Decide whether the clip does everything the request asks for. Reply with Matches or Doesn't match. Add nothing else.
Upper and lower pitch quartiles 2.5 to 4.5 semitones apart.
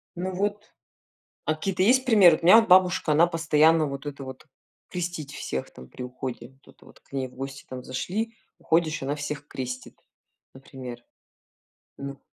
Doesn't match